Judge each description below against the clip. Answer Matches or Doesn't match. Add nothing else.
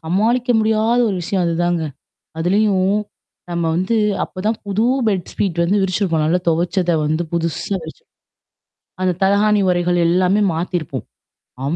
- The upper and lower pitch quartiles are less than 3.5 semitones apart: Matches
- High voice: Doesn't match